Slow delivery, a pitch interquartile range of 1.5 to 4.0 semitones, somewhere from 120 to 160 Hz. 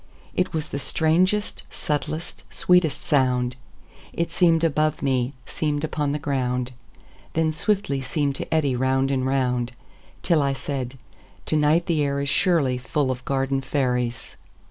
Yes: slow, 130 wpm; average, 3.4 semitones; medium, 140 Hz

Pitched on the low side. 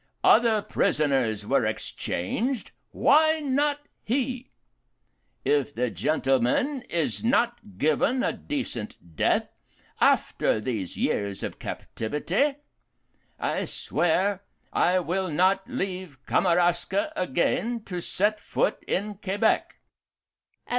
No: medium, 185 Hz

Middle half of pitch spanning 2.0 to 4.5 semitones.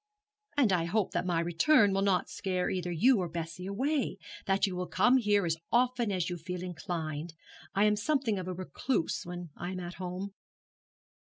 Yes: average, 3.1 semitones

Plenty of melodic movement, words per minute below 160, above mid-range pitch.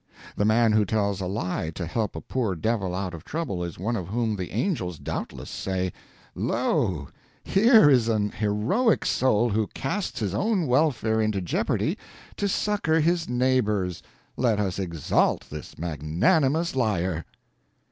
No: wide, 6.1 semitones; average, 150 wpm; low, 110 Hz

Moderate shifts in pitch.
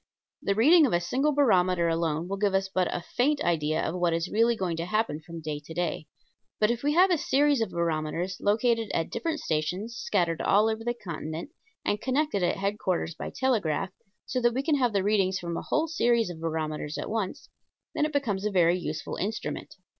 No: wide, 6.0 semitones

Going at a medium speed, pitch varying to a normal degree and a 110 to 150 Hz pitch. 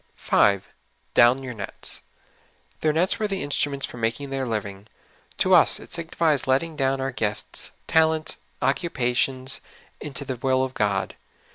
Yes: average, 150 wpm; average, 3.9 semitones; low, 135 Hz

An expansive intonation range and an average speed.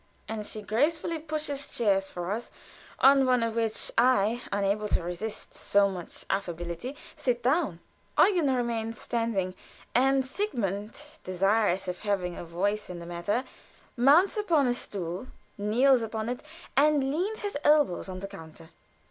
Yes: wide, 5.7 semitones; average, 150 wpm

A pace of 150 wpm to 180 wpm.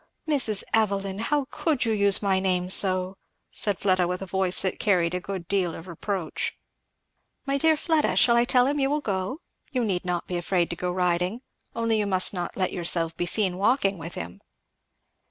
No: average, 195 wpm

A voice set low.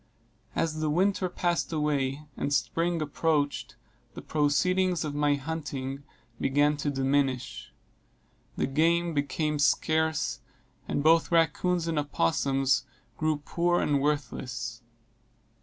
No: medium, 150 Hz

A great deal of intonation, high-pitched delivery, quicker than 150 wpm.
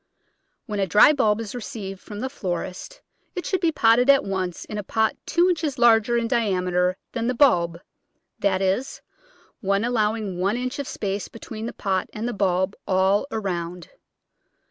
No: average, 4.2 semitones; high, 210 Hz; average, 170 wpm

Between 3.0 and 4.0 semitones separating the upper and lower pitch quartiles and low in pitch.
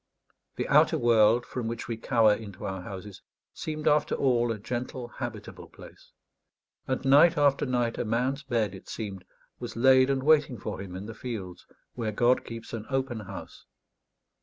Yes: average, 3.6 semitones; low, 120 Hz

